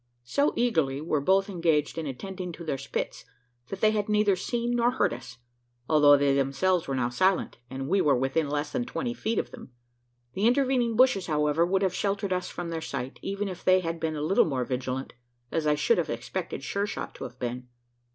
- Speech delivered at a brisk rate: Yes, fast, 210 wpm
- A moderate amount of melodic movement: No, wide, 6.2 semitones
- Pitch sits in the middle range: Yes, medium, 170 Hz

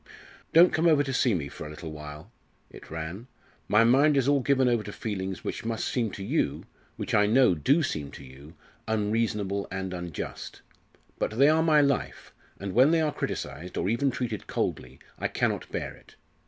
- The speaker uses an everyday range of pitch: No, wide, 7.1 semitones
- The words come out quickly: No, average, 195 wpm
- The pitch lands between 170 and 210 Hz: No, low, 110 Hz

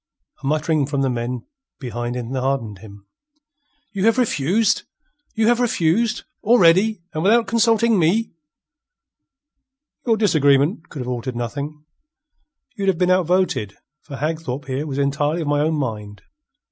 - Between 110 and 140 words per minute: Yes, slow, 135 wpm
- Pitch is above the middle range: No, medium, 155 Hz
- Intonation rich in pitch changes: Yes, wide, 6.9 semitones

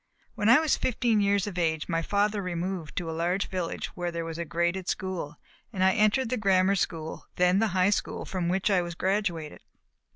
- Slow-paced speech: No, fast, 205 wpm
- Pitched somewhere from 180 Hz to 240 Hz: Yes, medium, 185 Hz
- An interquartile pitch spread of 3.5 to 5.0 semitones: No, average, 2.9 semitones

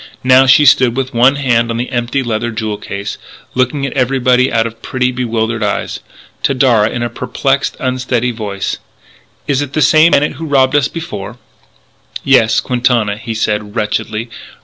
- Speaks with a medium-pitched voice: No, low, 125 Hz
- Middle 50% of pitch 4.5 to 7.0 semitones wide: No, average, 2.8 semitones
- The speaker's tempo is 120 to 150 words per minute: No, average, 170 wpm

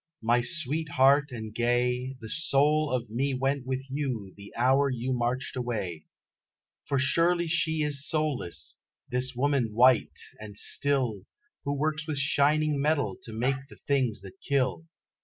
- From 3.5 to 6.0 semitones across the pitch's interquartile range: No, average, 3.1 semitones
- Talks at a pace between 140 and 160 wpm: Yes, average, 150 wpm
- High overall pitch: No, low, 130 Hz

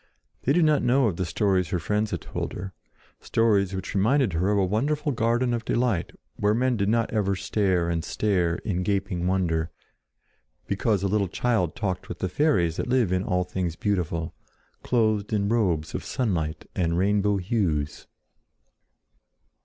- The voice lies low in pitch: Yes, low, 100 Hz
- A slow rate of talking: No, average, 165 wpm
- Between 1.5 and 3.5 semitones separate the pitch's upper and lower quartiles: No, average, 4.1 semitones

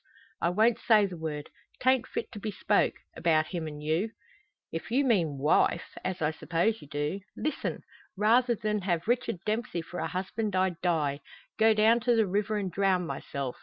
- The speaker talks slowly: No, average, 185 wpm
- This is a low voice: No, high, 190 Hz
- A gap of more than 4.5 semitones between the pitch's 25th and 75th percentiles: Yes, average, 5.2 semitones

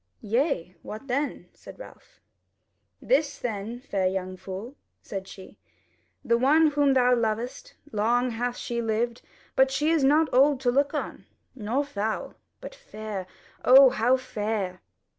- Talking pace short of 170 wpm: Yes, average, 140 wpm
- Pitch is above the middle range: Yes, high, 245 Hz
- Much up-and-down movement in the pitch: No, average, 4.5 semitones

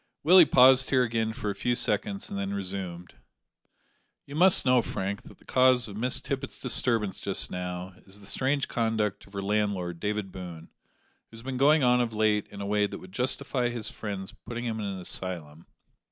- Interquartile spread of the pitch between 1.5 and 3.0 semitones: No, average, 4.3 semitones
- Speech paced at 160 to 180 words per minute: No, average, 195 wpm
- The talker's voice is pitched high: No, low, 105 Hz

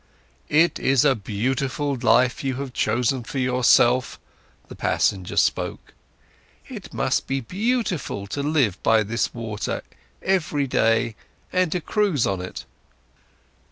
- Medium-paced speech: No, slow, 120 wpm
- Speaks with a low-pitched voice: Yes, low, 130 Hz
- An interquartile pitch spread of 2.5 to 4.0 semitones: No, average, 4.4 semitones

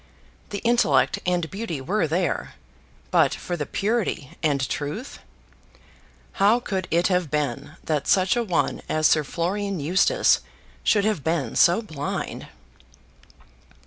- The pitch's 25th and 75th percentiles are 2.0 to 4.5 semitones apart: No, average, 5.1 semitones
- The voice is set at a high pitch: No, medium, 175 Hz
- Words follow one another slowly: Yes, slow, 130 wpm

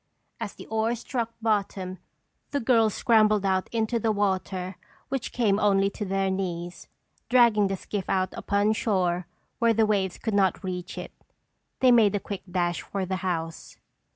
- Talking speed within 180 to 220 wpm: No, average, 165 wpm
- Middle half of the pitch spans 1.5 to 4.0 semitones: Yes, average, 2.9 semitones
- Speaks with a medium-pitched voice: No, high, 200 Hz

